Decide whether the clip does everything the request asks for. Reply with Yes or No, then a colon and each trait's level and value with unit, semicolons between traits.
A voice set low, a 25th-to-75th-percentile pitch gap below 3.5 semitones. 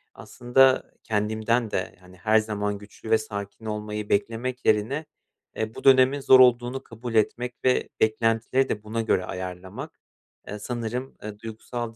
Yes: low, 110 Hz; narrow, 2.6 semitones